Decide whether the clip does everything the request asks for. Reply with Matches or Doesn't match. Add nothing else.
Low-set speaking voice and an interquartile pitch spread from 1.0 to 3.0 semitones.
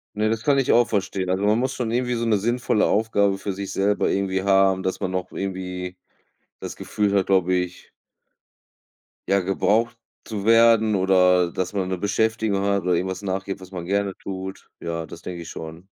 Matches